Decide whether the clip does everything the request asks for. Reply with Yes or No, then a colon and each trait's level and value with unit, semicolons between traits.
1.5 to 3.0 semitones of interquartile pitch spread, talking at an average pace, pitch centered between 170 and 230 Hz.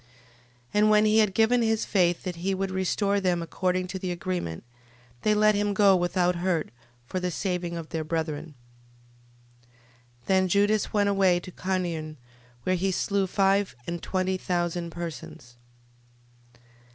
Yes: narrow, 2.5 semitones; average, 155 wpm; medium, 185 Hz